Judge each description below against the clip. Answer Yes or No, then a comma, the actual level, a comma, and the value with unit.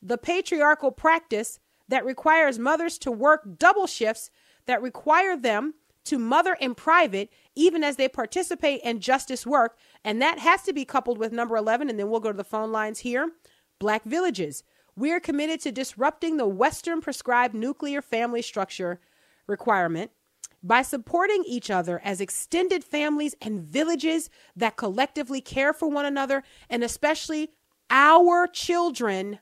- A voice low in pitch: No, very high, 270 Hz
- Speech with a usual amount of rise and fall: No, wide, 5.7 semitones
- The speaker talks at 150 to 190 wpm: Yes, average, 155 wpm